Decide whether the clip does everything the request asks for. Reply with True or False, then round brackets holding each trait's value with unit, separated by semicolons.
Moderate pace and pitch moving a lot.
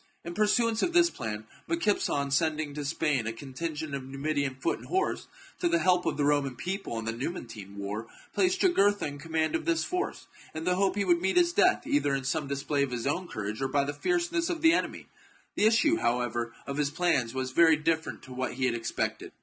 False (220 wpm; 7.7 semitones)